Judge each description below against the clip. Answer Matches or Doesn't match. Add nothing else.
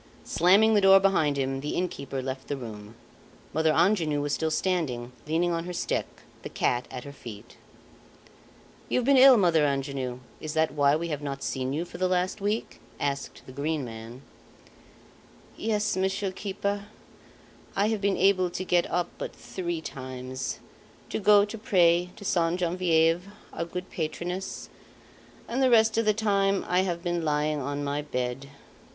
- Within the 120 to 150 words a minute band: Doesn't match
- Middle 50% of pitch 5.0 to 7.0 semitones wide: Matches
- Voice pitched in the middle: Matches